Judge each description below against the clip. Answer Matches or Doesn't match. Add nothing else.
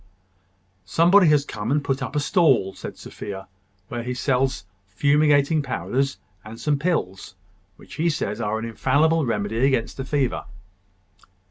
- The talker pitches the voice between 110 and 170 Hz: Matches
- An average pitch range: Matches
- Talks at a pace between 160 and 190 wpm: Doesn't match